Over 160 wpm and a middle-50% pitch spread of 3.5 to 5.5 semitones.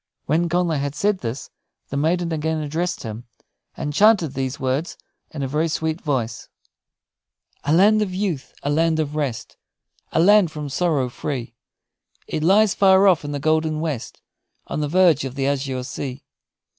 Yes: average, 170 wpm; average, 3.9 semitones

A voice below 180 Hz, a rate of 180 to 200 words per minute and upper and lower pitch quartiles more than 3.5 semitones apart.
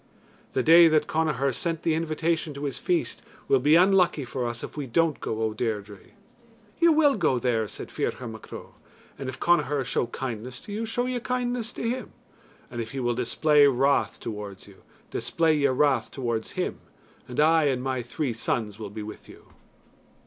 Yes: medium, 140 Hz; average, 190 wpm; wide, 5.6 semitones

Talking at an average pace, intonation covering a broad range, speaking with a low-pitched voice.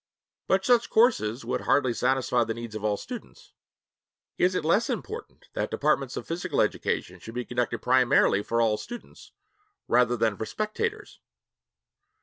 Yes: average, 150 wpm; wide, 8.9 semitones; low, 125 Hz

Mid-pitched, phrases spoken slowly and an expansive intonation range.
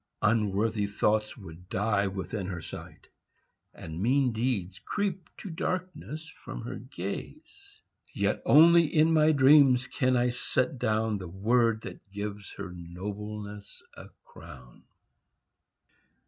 No: low, 110 Hz; slow, 120 wpm; wide, 6.1 semitones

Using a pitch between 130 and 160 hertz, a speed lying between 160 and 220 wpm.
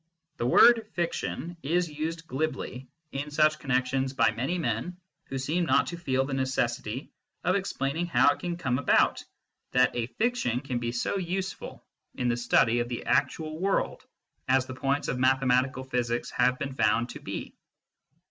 Yes: low, 135 Hz; average, 175 wpm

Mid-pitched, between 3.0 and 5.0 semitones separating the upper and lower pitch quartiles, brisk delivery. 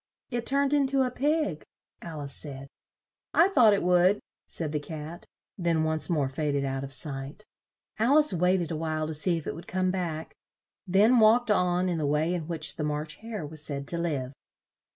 No: medium, 170 Hz; wide, 5.5 semitones; fast, 210 wpm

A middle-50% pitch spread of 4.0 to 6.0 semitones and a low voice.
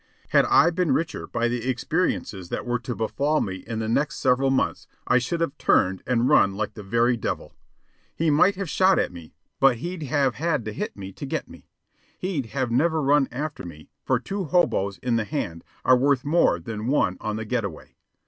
Yes: wide, 5.6 semitones; low, 125 Hz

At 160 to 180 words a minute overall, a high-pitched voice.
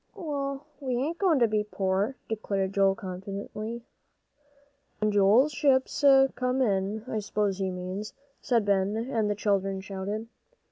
No: average, 140 wpm; high, 210 Hz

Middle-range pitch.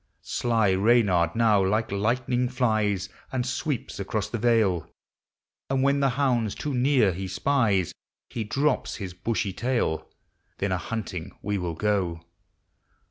No: low, 110 Hz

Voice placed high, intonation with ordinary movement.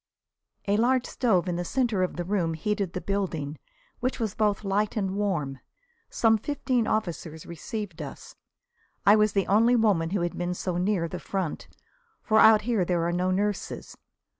Yes: high, 195 Hz; average, 3.6 semitones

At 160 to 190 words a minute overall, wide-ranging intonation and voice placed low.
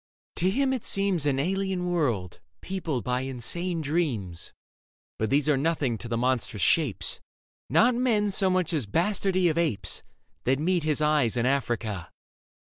No: average, 165 wpm; wide, 6.8 semitones; medium, 155 Hz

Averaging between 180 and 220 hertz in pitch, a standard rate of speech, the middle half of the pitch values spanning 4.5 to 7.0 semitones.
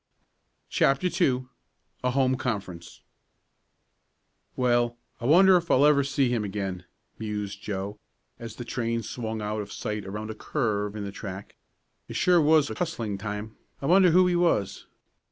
No: low, 115 Hz; average, 155 wpm; average, 5.1 semitones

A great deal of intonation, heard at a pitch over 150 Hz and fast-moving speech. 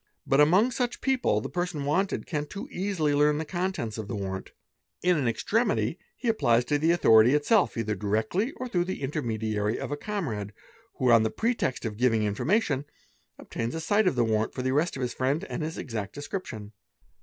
No: wide, 8.4 semitones; medium, 145 Hz; fast, 215 wpm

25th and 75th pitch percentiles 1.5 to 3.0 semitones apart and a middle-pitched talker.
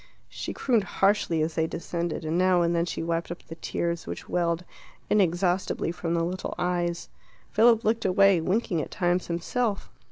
Yes: narrow, 2.4 semitones; medium, 175 Hz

